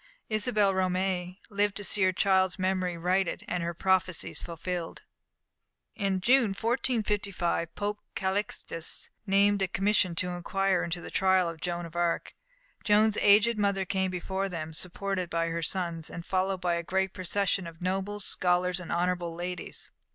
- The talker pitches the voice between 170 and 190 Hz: Yes, medium, 185 Hz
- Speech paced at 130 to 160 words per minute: Yes, average, 155 wpm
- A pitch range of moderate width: No, narrow, 2.2 semitones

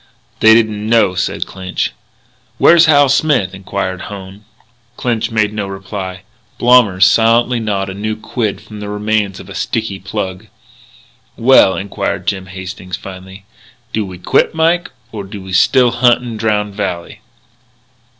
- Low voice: Yes, low, 105 Hz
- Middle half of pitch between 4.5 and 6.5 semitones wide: No, average, 3.1 semitones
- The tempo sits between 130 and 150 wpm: Yes, average, 145 wpm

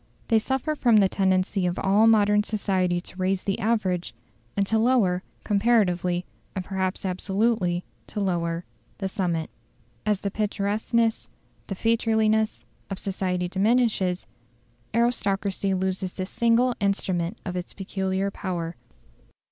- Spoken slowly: Yes, slow, 125 wpm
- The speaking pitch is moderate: No, high, 195 Hz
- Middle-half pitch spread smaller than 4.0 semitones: Yes, average, 2.9 semitones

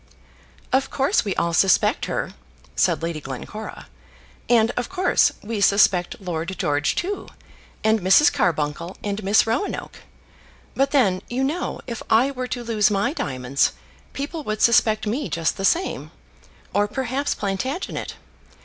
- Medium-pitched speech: No, high, 215 Hz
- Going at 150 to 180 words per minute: No, average, 140 wpm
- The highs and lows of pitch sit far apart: Yes, wide, 6.3 semitones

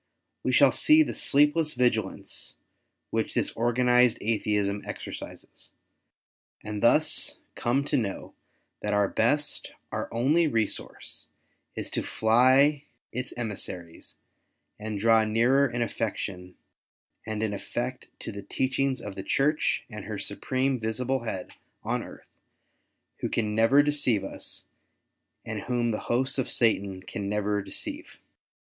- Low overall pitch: Yes, low, 115 Hz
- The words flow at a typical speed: No, slow, 130 wpm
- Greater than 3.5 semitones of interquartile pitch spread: Yes, average, 3.9 semitones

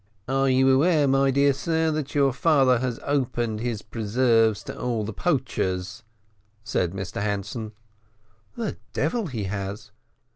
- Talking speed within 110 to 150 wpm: Yes, average, 140 wpm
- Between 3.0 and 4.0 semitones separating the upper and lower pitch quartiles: No, average, 4.7 semitones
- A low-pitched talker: Yes, low, 125 Hz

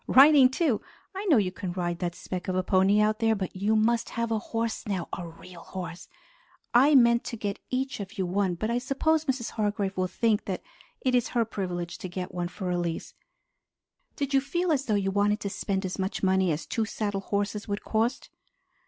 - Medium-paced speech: No, fast, 215 wpm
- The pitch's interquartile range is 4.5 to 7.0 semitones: No, average, 4.1 semitones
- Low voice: No, high, 205 Hz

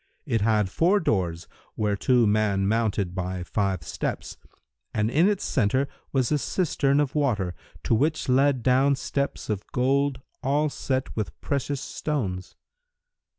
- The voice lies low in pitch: Yes, low, 125 Hz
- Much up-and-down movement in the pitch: Yes, wide, 5.7 semitones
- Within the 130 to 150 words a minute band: Yes, average, 140 wpm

